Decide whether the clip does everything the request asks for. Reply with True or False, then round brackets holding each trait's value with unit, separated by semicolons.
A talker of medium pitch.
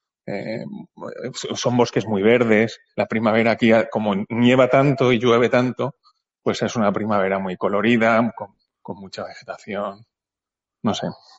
False (115 Hz)